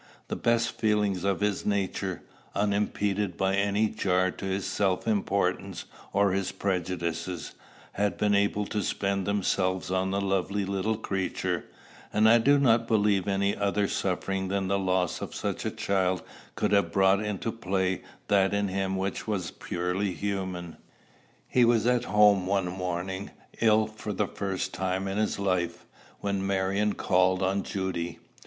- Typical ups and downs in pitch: No, narrow, 1.6 semitones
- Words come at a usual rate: Yes, average, 155 wpm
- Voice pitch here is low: Yes, low, 100 Hz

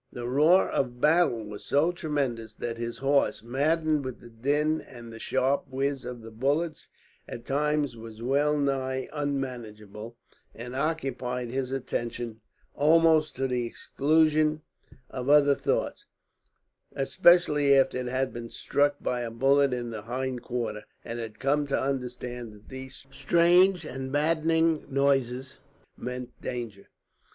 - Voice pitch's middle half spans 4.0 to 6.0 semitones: No, average, 3.6 semitones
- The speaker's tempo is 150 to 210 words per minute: No, average, 140 wpm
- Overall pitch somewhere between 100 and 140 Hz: Yes, low, 135 Hz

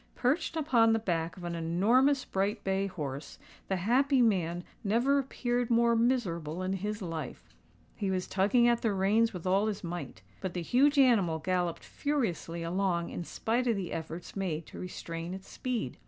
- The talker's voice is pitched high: Yes, high, 195 Hz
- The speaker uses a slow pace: No, average, 175 wpm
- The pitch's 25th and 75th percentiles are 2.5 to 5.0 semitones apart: No, wide, 5.5 semitones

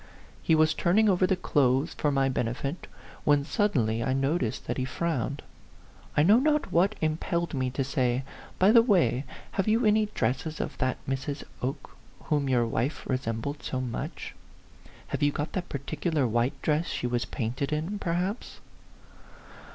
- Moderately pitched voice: Yes, medium, 145 Hz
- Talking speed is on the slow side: No, average, 165 wpm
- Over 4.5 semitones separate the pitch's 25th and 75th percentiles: Yes, average, 5.2 semitones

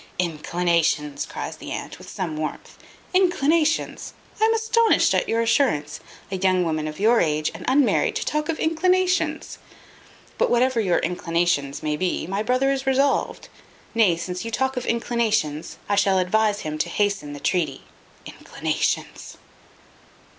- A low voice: No, high, 205 Hz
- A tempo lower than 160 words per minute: Yes, average, 150 wpm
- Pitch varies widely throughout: Yes, wide, 8.1 semitones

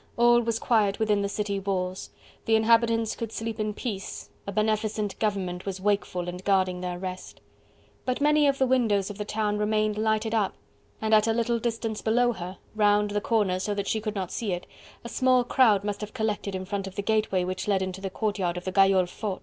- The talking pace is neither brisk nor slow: No, fast, 215 wpm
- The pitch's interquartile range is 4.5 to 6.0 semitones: No, narrow, 2.5 semitones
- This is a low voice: No, high, 210 Hz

